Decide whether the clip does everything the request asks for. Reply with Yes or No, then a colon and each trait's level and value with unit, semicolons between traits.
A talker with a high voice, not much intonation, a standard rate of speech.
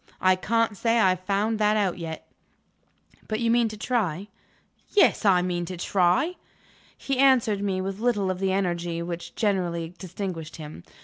No: high, 195 Hz; average, 3.7 semitones; average, 170 wpm